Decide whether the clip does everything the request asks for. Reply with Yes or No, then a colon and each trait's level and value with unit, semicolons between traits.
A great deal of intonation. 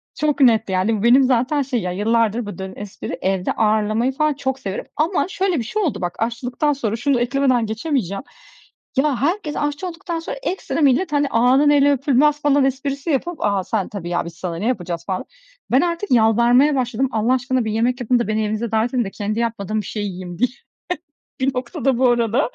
No: average, 4.6 semitones